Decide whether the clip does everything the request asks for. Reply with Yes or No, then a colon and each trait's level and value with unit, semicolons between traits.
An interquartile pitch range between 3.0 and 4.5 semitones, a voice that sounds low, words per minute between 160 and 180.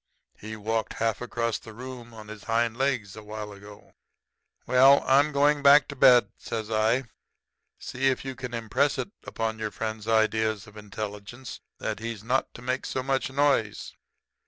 Yes: average, 3.3 semitones; low, 115 Hz; average, 170 wpm